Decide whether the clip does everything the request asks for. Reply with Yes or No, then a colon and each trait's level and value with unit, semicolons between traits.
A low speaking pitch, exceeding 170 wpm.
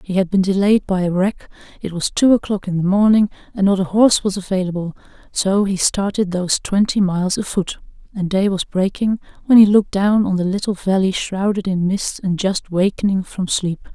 No: high, 195 Hz; average, 200 wpm